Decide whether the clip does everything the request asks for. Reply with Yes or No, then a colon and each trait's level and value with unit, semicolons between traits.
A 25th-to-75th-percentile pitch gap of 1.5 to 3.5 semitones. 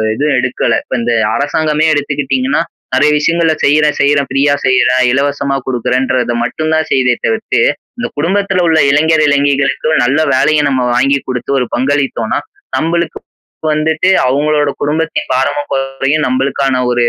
Yes: average, 2.8 semitones